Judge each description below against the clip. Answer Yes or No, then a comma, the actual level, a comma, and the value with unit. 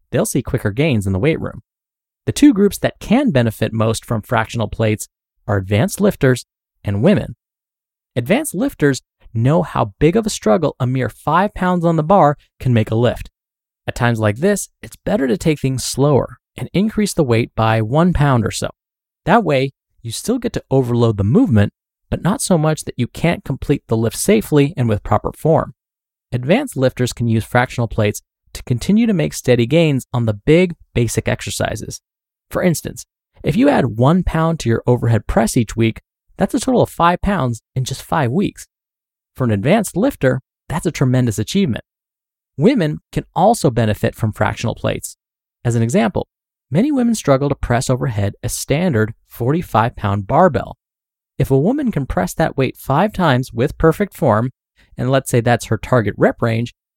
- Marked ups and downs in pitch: Yes, wide, 6.3 semitones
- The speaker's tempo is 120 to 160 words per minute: No, average, 185 wpm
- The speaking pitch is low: Yes, low, 125 Hz